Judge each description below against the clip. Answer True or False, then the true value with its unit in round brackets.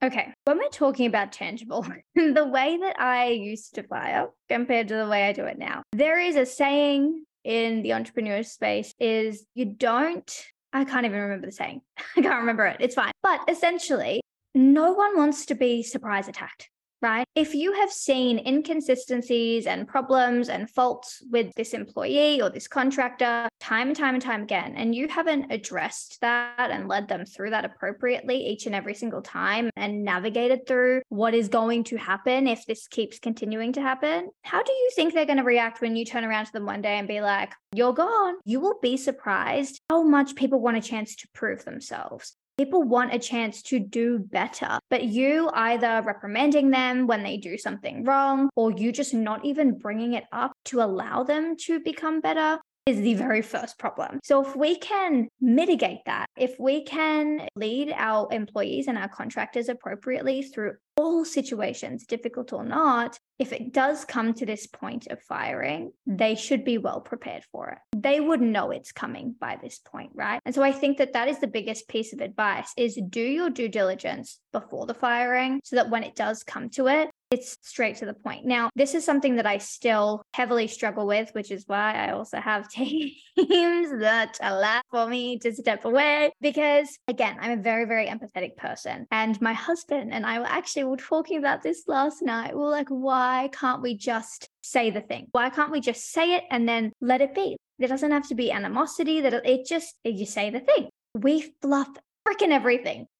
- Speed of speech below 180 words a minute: False (195 wpm)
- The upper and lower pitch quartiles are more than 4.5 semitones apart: False (4.0 semitones)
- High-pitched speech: True (250 Hz)